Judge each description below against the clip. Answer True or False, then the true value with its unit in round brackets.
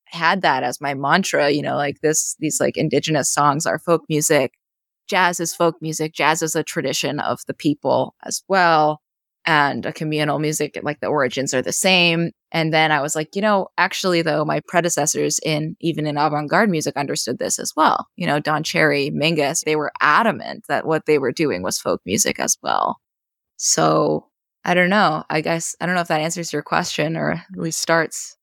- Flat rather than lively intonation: True (2.1 semitones)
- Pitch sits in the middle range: True (155 Hz)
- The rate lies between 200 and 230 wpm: True (205 wpm)